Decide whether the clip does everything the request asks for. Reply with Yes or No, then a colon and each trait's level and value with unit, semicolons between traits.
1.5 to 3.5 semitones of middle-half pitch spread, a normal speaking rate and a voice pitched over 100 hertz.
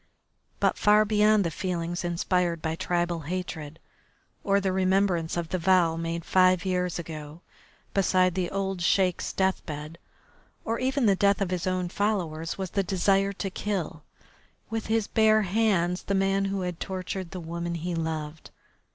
Yes: narrow, 2.6 semitones; average, 160 wpm; medium, 185 Hz